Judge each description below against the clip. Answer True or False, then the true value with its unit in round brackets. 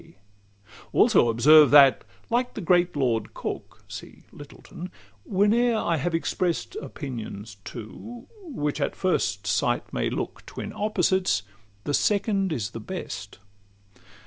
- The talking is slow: True (120 wpm)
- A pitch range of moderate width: False (8.8 semitones)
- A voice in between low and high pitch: True (160 Hz)